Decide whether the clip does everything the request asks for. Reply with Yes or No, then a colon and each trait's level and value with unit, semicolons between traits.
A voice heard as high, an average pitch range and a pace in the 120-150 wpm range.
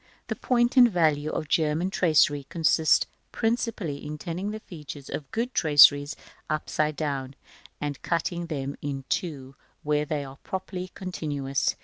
No: medium, 155 Hz; average, 4.0 semitones; average, 145 wpm